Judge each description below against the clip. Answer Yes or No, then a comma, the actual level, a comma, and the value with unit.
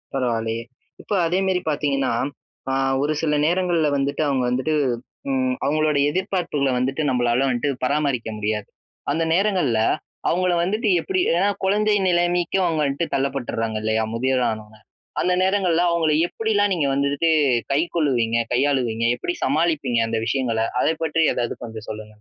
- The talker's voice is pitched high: No, medium, 140 Hz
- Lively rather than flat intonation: Yes, wide, 5.9 semitones